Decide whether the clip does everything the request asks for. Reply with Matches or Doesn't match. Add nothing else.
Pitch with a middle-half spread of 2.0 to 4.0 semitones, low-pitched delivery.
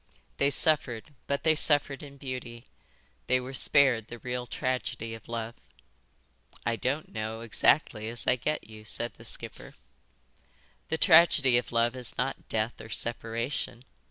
Matches